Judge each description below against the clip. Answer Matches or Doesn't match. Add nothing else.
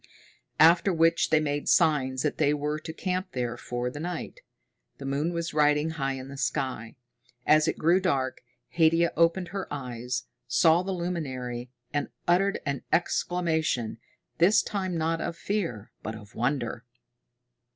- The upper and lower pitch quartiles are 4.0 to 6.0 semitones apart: Matches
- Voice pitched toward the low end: Doesn't match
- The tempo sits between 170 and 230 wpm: Doesn't match